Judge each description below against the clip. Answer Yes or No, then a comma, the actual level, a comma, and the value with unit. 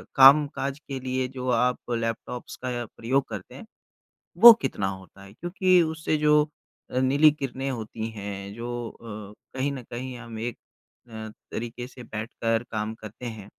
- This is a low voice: Yes, low, 120 Hz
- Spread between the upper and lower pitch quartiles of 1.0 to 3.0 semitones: No, average, 3.4 semitones